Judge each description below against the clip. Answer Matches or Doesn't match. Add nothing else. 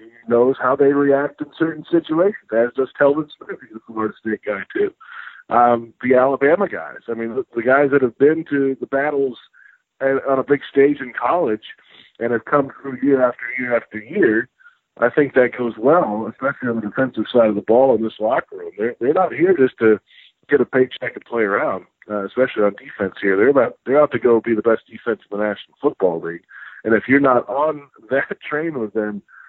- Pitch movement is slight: Doesn't match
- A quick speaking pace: Matches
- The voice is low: Matches